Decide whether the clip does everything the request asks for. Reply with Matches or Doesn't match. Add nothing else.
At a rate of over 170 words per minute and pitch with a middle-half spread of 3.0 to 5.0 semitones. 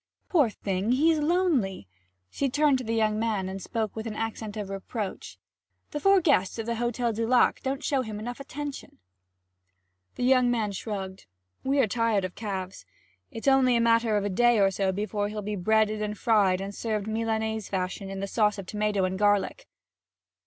Matches